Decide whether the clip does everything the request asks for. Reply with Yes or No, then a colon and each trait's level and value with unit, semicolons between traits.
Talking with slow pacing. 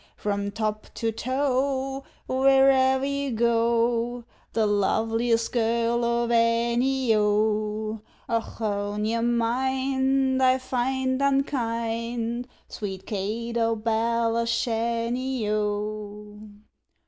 Yes: slow, 85 wpm